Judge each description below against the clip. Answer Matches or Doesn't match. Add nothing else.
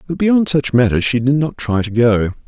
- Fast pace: Matches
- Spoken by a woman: Doesn't match